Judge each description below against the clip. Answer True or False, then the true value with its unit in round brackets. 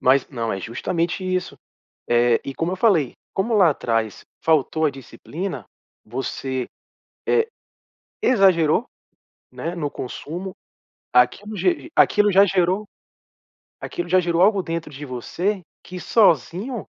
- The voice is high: False (170 Hz)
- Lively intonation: True (6.3 semitones)